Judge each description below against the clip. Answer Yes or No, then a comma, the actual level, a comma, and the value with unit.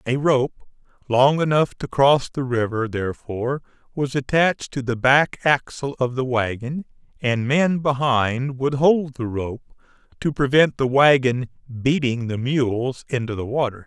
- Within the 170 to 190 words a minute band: No, average, 150 wpm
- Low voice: Yes, low, 130 Hz